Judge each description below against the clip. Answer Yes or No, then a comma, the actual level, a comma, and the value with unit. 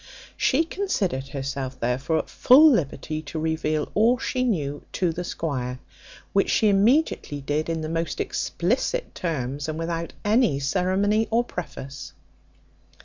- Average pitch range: No, wide, 7.0 semitones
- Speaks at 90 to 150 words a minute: Yes, average, 140 wpm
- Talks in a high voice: No, medium, 165 Hz